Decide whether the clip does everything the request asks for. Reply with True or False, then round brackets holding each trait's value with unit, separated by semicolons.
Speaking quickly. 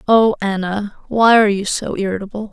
False (165 wpm)